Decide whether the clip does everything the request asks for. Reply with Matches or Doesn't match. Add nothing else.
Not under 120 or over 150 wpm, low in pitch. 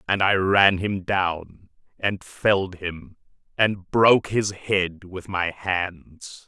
Matches